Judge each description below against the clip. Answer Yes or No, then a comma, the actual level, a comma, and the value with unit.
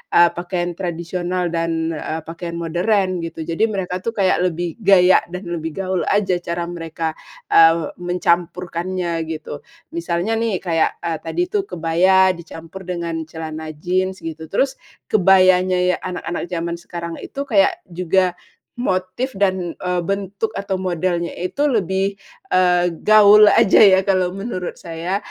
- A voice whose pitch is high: No, medium, 180 Hz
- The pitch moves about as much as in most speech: No, narrow, 2.1 semitones